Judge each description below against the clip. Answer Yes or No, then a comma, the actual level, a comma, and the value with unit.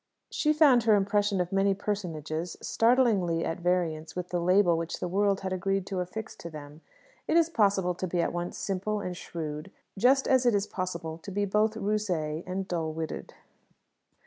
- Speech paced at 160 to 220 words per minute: Yes, average, 185 wpm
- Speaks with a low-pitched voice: No, medium, 185 Hz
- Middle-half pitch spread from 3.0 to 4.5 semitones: Yes, average, 3.4 semitones